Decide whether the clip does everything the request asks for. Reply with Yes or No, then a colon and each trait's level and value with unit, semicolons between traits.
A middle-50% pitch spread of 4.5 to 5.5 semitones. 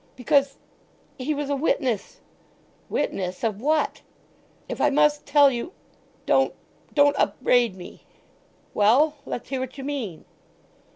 No: average, 3.6 semitones